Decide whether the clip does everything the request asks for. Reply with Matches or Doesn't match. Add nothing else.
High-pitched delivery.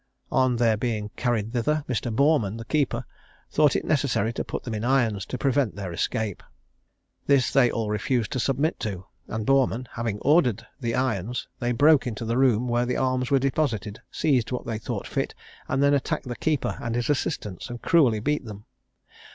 Doesn't match